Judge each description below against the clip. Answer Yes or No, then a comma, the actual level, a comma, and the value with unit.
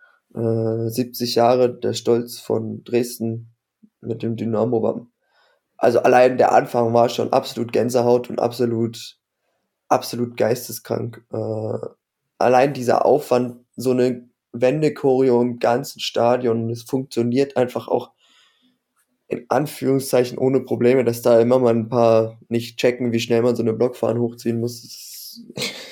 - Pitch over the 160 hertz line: No, low, 120 Hz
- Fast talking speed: No, average, 130 wpm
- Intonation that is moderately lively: No, narrow, 1.5 semitones